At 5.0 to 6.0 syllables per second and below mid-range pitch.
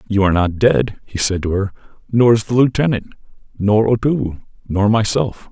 Yes: 5.4 syllables/s; low, 110 Hz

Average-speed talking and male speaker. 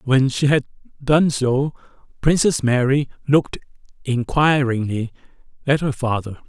No: slow, 110 wpm; male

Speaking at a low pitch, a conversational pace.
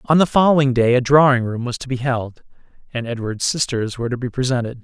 No: low, 125 Hz; fast, 225 wpm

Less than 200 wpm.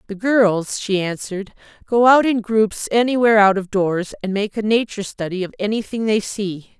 Yes: average, 185 wpm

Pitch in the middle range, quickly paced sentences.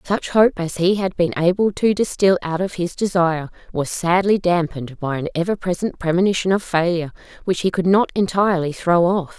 No: medium, 180 Hz; average, 190 wpm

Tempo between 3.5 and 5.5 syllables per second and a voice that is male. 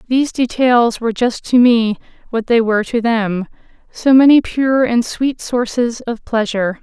No: 4.6 syllables/s; female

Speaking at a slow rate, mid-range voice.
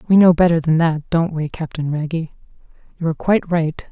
No: average, 200 wpm; medium, 165 Hz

